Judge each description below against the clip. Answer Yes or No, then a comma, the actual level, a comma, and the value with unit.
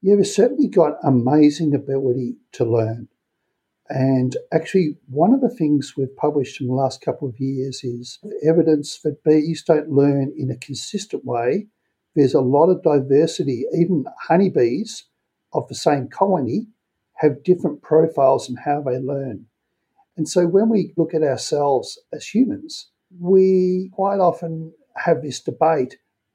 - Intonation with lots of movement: Yes, wide, 5.7 semitones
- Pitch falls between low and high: Yes, medium, 155 Hz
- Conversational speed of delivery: Yes, average, 150 wpm